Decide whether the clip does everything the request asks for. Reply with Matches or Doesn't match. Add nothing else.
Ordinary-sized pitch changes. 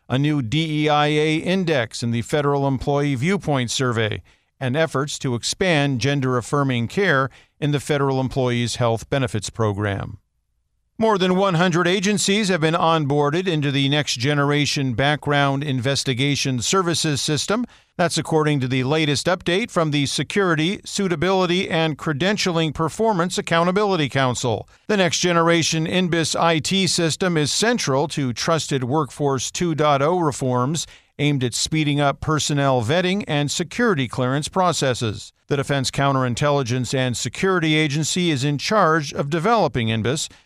Matches